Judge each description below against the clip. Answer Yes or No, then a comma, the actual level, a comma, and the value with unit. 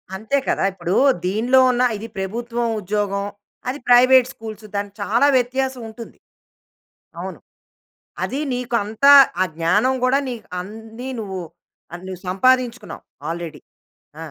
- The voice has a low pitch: No, high, 225 Hz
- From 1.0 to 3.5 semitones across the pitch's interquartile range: No, average, 4.1 semitones